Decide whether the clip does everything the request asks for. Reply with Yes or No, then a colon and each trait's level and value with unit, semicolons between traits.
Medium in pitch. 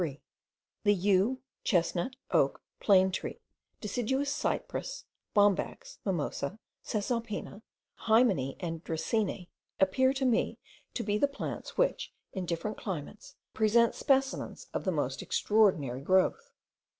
No: high, 205 Hz